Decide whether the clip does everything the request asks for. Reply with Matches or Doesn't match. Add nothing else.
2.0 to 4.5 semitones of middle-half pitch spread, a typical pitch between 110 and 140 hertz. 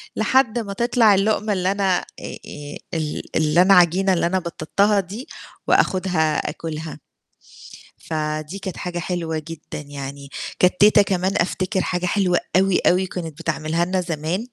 Doesn't match